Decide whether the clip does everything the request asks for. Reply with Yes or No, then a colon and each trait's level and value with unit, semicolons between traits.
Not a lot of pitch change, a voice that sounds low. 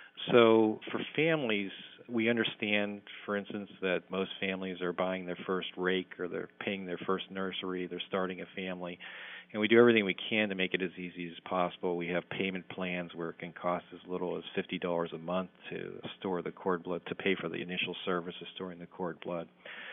Yes: narrow, 2.1 semitones; very low, 95 Hz